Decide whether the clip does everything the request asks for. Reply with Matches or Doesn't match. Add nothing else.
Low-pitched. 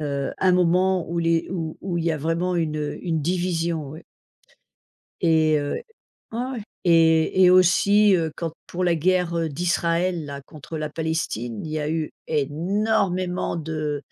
Doesn't match